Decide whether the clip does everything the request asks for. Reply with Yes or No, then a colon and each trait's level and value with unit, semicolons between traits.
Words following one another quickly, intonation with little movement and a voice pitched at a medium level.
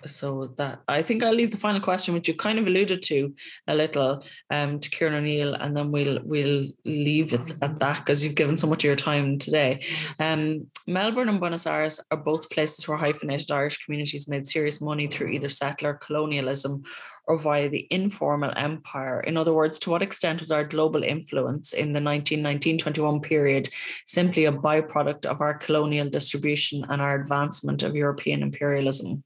No: average, 185 wpm; narrow, 1.8 semitones; medium, 150 Hz